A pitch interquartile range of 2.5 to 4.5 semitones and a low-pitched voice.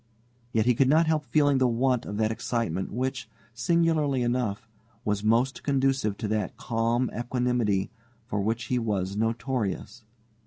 Yes: average, 3.3 semitones; low, 120 Hz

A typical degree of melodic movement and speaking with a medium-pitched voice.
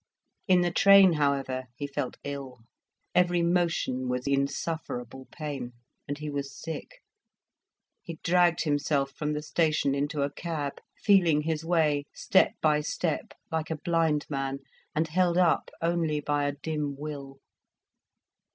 Yes: average, 3.0 semitones; medium, 150 Hz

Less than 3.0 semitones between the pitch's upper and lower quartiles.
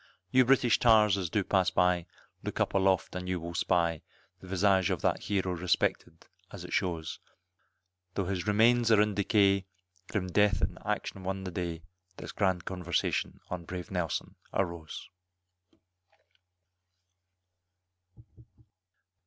Yes: narrow, 2.4 semitones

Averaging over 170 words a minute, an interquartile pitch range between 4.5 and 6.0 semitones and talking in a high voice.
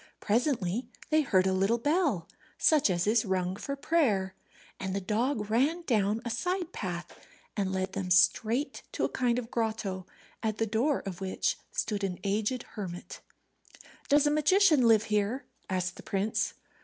No: average, 165 wpm; wide, 5.6 semitones; high, 215 Hz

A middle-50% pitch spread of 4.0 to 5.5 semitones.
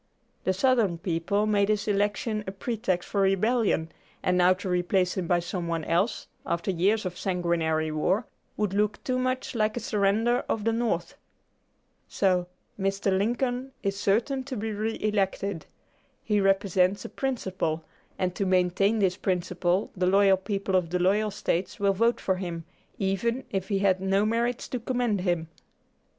No: average, 3.0 semitones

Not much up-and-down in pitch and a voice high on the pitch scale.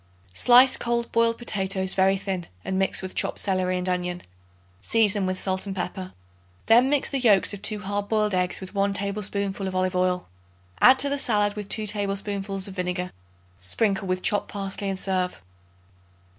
Yes: narrow, 2.1 semitones; high, 195 Hz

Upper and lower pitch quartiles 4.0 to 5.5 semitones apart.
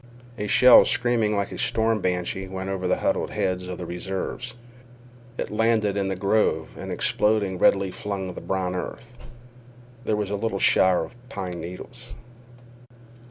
No: average, 3.2 semitones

